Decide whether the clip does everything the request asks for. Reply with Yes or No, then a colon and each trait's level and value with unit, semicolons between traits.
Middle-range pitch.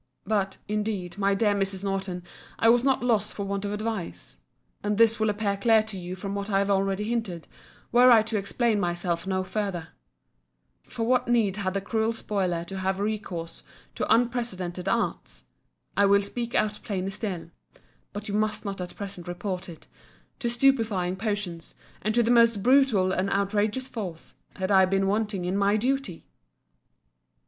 No: high, 200 Hz